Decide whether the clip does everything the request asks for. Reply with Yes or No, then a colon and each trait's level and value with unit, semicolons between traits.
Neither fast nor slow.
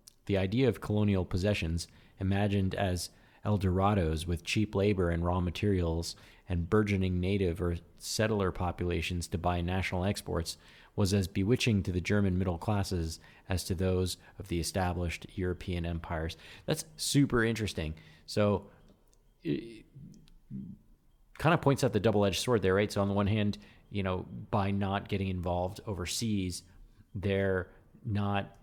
Yes: average, 145 wpm